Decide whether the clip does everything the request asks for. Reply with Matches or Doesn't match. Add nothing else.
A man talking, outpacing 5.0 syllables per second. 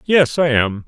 Doesn't match